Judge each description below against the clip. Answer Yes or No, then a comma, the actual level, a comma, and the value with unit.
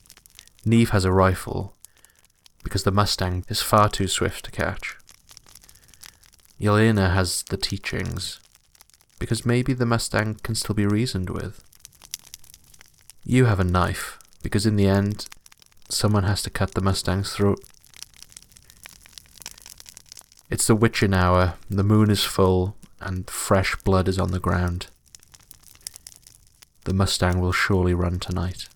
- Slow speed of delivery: Yes, slow, 130 wpm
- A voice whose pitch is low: Yes, very low, 95 Hz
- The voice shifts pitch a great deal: No, average, 2.7 semitones